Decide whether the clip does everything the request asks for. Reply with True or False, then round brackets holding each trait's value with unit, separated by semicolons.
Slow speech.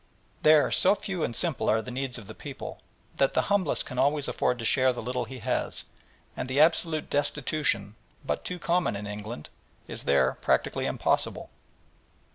False (175 wpm)